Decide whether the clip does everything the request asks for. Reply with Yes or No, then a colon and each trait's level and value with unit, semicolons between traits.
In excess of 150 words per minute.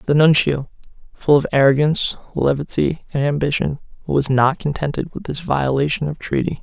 No: average, 145 wpm